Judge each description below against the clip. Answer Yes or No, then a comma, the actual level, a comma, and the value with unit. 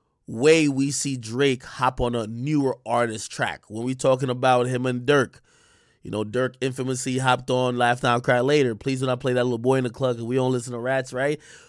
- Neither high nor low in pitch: No, low, 130 Hz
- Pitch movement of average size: No, narrow, 1.5 semitones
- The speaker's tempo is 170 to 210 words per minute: No, fast, 220 wpm